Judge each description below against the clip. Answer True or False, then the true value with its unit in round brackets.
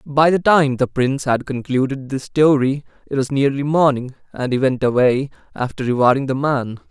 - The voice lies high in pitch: False (135 Hz)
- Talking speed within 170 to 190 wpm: True (180 wpm)